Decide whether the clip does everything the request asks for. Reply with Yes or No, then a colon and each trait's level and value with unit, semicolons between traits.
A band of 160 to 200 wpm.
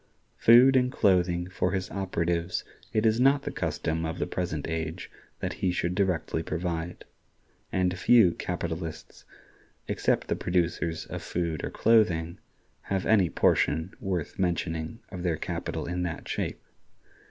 No: average, 140 wpm